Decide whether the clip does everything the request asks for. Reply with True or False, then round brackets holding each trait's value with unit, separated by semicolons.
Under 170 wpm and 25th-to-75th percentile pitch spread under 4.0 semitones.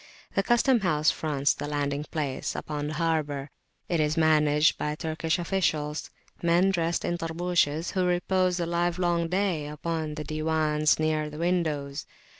True (150 wpm; 2.5 semitones)